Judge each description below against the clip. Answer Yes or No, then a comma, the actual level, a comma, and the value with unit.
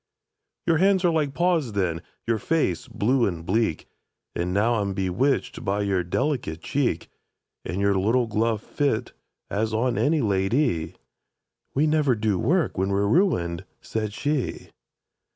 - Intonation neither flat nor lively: No, wide, 6.7 semitones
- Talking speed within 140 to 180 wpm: Yes, average, 150 wpm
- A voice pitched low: Yes, low, 110 Hz